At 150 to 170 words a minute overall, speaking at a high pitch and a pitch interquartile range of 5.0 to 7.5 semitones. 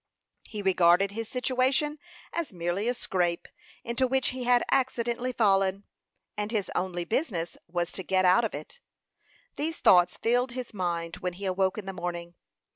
Yes: average, 165 wpm; high, 200 Hz; wide, 5.6 semitones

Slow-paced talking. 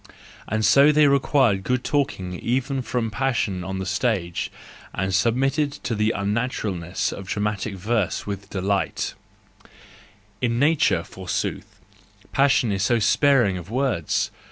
Yes: slow, 130 wpm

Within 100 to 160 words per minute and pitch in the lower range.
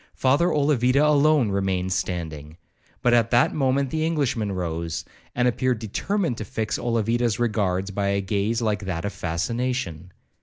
Yes: average, 150 wpm; low, 110 Hz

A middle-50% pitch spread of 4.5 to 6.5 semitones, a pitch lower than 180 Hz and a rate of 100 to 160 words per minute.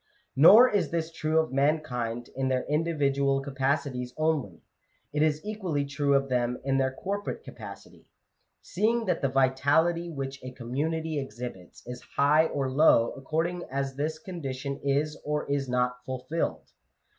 No: average, 3.3 semitones; medium, 140 Hz; average, 145 wpm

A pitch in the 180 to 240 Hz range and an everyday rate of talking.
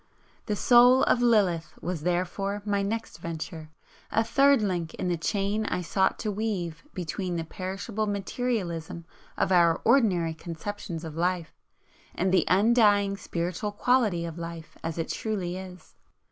Yes: medium, 185 Hz; average, 145 wpm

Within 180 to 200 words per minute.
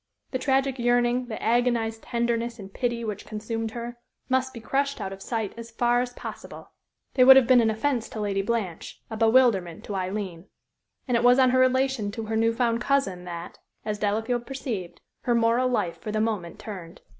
Yes: average, 195 wpm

